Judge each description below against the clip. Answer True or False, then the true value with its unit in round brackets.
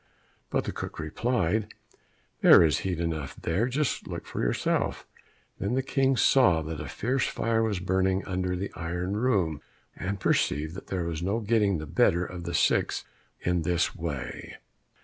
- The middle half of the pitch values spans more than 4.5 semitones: True (4.9 semitones)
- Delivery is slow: False (165 wpm)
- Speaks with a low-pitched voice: True (90 Hz)